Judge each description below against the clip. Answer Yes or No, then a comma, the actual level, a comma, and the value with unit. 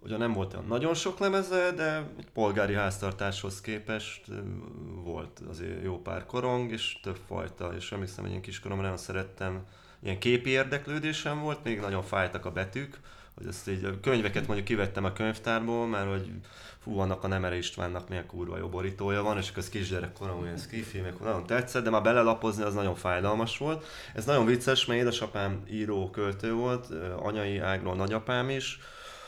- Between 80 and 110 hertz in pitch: Yes, low, 100 Hz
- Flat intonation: No, average, 3.9 semitones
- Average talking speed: No, fast, 170 wpm